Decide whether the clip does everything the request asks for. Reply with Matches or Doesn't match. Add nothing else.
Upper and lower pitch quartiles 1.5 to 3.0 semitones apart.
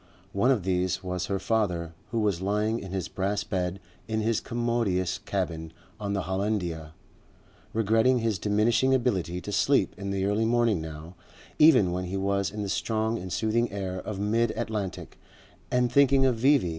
Doesn't match